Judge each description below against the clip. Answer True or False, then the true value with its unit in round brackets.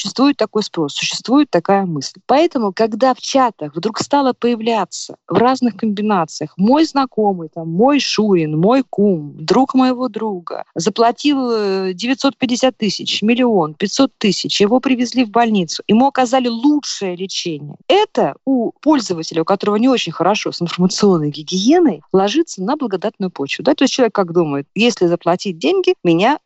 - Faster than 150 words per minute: False (145 wpm)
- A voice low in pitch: False (215 Hz)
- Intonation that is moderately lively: False (6.1 semitones)